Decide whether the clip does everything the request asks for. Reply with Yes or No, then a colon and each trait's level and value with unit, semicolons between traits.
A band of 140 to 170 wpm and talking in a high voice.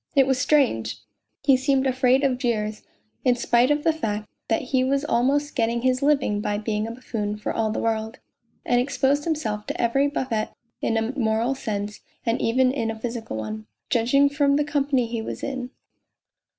No: average, 185 wpm; high, 245 Hz